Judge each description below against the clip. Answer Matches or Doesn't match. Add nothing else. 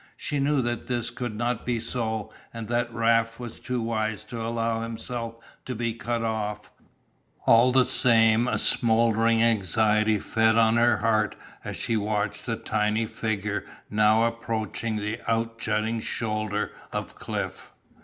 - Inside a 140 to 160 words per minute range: Matches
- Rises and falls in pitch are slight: Matches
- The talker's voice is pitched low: Matches